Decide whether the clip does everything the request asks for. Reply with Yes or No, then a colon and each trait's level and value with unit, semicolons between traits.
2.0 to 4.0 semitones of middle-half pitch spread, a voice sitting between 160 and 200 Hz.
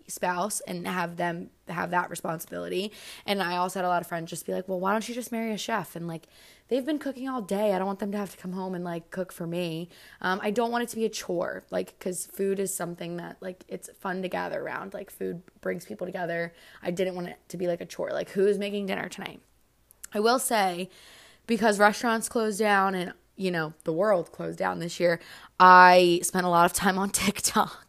Yes: average, 2.9 semitones; medium, 185 Hz